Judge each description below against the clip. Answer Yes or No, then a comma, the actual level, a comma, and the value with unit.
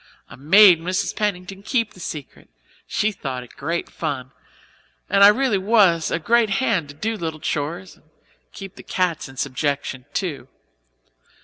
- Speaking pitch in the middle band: Yes, medium, 175 Hz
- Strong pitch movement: Yes, wide, 5.7 semitones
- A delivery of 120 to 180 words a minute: Yes, average, 155 wpm